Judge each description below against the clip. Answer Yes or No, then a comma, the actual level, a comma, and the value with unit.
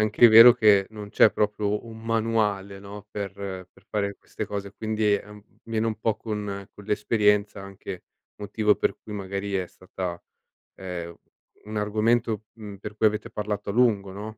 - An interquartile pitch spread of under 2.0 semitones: Yes, narrow, 1.6 semitones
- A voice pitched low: Yes, low, 105 Hz